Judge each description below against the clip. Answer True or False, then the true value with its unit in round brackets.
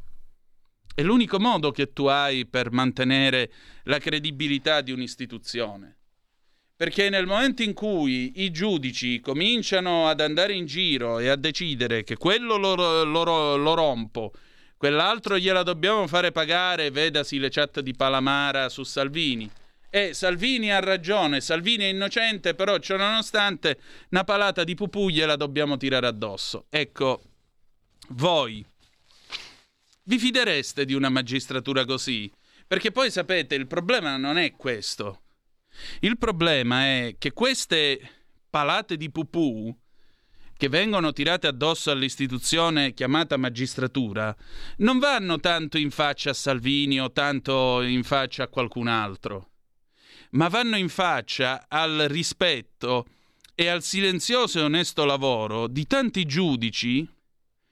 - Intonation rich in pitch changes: True (6.1 semitones)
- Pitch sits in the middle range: True (150 Hz)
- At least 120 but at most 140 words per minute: True (130 wpm)